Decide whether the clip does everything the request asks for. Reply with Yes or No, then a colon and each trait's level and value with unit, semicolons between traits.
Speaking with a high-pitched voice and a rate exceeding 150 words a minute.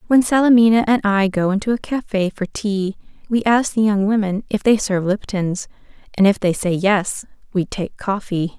Yes: high, 205 Hz; average, 190 wpm